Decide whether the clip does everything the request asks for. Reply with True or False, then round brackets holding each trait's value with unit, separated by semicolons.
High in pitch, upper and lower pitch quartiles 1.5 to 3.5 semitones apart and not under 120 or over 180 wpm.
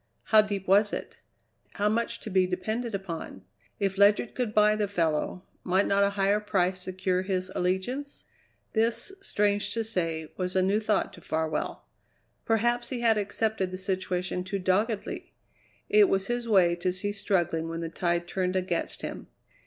True (195 Hz; 2.8 semitones; 170 wpm)